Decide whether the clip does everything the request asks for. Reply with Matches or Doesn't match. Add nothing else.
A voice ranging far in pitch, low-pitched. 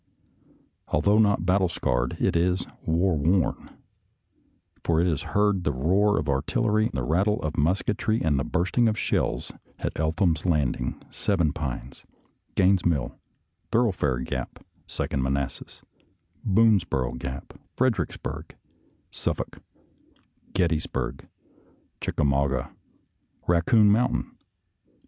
Matches